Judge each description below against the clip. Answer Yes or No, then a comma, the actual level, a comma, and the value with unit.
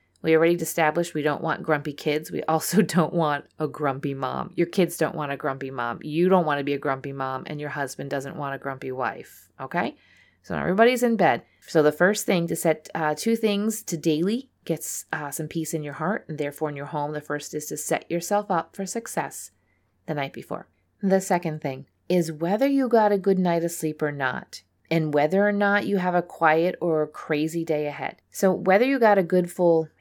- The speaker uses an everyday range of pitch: Yes, average, 3.6 semitones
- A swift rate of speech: Yes, fast, 225 wpm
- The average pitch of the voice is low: No, medium, 160 Hz